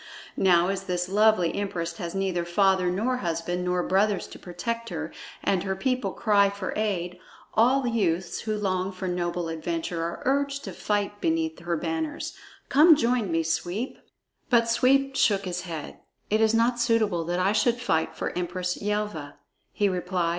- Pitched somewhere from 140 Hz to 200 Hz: Yes, high, 190 Hz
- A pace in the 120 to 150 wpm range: No, average, 170 wpm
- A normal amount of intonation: Yes, average, 4.1 semitones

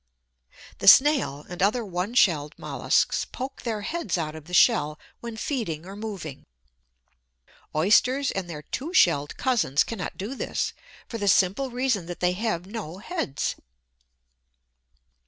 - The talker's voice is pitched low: No, high, 195 Hz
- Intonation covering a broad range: Yes, wide, 6.4 semitones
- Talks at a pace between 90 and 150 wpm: Yes, average, 140 wpm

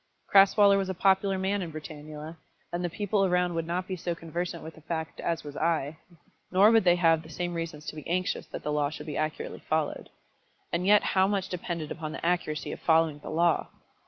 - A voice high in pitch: No, medium, 170 Hz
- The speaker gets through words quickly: Yes, fast, 215 wpm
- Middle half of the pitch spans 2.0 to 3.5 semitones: Yes, average, 2.9 semitones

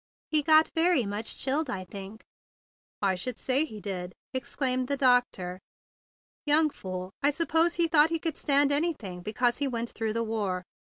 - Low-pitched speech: No, very high, 255 Hz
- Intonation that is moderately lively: No, wide, 6.9 semitones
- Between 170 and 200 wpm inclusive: Yes, average, 175 wpm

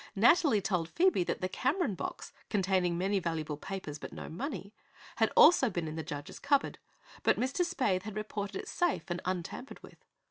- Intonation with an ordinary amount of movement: No, wide, 6.8 semitones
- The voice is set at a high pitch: Yes, high, 195 Hz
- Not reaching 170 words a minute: No, average, 180 wpm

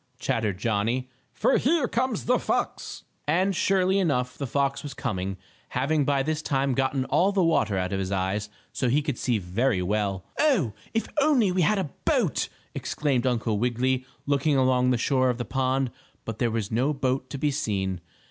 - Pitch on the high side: No, low, 130 Hz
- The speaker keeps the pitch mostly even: No, average, 5.0 semitones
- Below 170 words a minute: No, average, 185 wpm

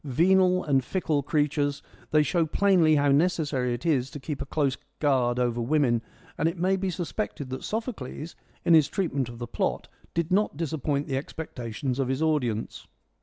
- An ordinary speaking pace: Yes, average, 180 wpm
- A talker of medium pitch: Yes, medium, 145 Hz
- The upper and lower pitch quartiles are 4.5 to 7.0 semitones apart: No, average, 4.1 semitones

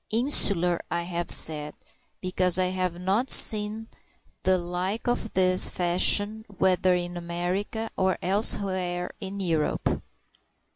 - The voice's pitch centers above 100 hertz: Yes, medium, 185 Hz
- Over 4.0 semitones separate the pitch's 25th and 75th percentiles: No, narrow, 2.4 semitones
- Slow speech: Yes, slow, 115 wpm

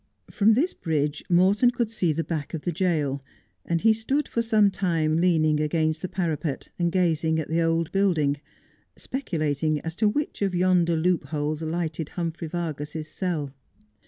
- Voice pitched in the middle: Yes, medium, 165 Hz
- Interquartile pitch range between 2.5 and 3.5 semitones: Yes, average, 3.2 semitones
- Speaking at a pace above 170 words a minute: No, average, 160 wpm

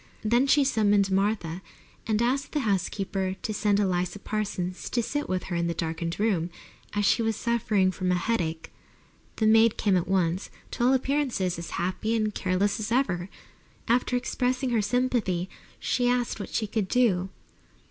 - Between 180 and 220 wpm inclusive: No, average, 170 wpm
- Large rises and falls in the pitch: No, average, 4.2 semitones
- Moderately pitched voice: No, high, 205 Hz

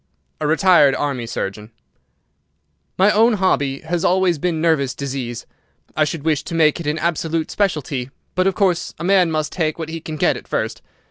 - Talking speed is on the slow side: No, average, 185 wpm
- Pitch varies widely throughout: No, average, 3.9 semitones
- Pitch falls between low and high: Yes, medium, 160 Hz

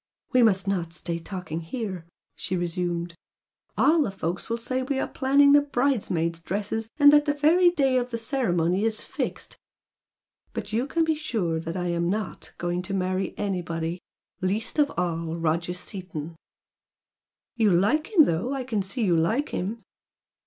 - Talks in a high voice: Yes, high, 195 Hz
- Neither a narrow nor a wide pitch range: No, wide, 6.9 semitones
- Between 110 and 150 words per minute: No, average, 165 wpm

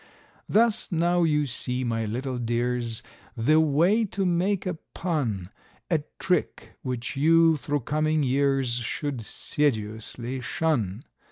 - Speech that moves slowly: Yes, slow, 120 wpm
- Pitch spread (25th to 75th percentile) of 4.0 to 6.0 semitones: Yes, wide, 5.4 semitones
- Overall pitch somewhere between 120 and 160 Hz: Yes, medium, 140 Hz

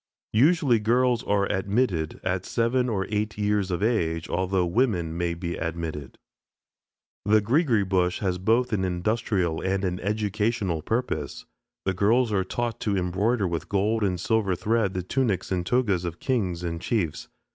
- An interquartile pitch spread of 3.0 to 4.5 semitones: Yes, average, 4.1 semitones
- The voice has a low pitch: Yes, low, 100 Hz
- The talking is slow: No, average, 155 wpm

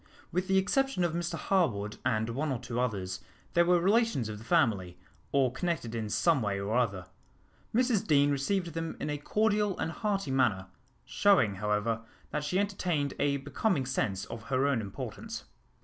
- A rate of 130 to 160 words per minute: No, average, 175 wpm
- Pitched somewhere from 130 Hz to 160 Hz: Yes, medium, 140 Hz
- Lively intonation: Yes, wide, 8.2 semitones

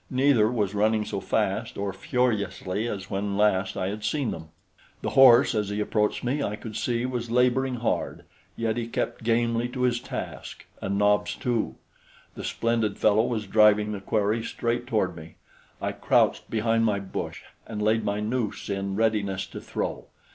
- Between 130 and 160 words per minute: No, average, 175 wpm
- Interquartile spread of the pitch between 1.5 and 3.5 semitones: Yes, narrow, 2.6 semitones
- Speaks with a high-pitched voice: No, low, 110 Hz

